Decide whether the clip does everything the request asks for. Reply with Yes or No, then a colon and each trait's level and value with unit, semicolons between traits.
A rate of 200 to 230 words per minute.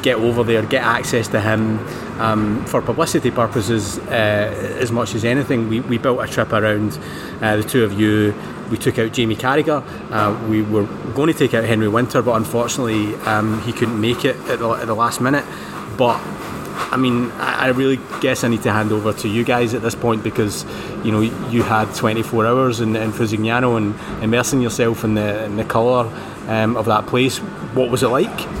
Yes: fast, 205 wpm